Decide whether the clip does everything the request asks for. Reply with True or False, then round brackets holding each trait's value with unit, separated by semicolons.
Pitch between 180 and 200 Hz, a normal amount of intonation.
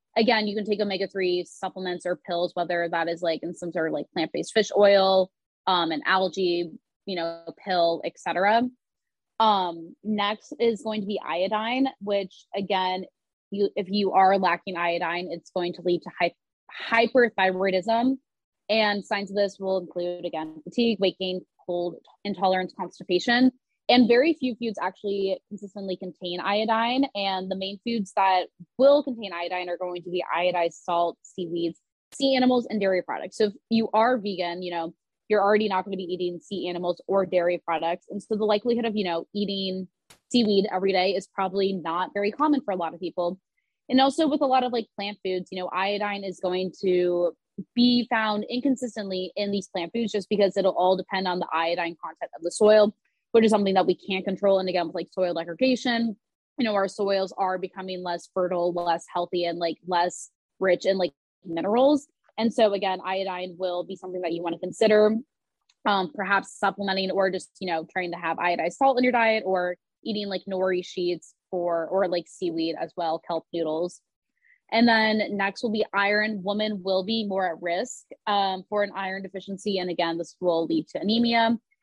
True (190 Hz; 3.1 semitones)